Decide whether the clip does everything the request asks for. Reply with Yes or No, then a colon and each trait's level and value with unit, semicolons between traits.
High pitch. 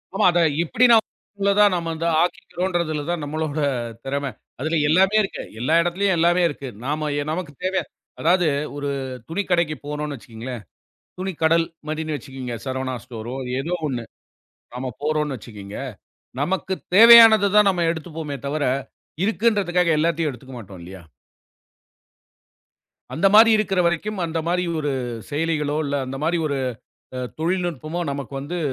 No: medium, 160 Hz